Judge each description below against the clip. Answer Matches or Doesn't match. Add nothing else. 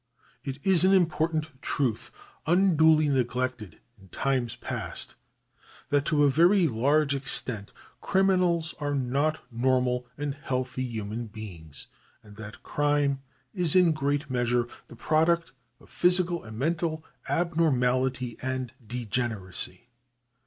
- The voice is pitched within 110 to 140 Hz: Matches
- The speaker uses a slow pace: Matches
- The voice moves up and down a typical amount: Matches